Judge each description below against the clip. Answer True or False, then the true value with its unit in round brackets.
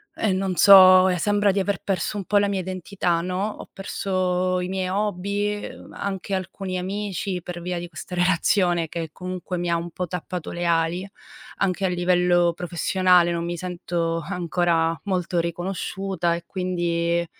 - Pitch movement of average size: False (1.8 semitones)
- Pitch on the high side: False (180 Hz)